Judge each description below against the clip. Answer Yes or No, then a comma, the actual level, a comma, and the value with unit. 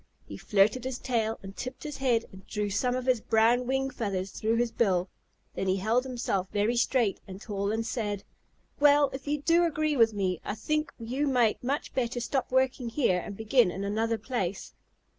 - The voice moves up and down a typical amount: Yes, average, 4.1 semitones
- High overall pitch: Yes, high, 230 Hz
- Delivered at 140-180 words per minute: No, average, 200 wpm